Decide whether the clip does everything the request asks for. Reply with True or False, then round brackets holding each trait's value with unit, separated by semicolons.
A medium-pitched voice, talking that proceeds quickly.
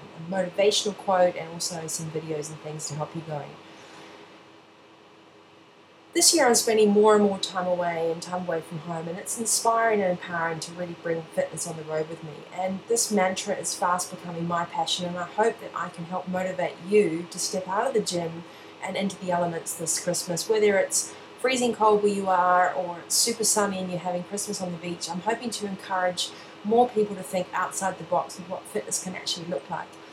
True (180 Hz; 210 wpm)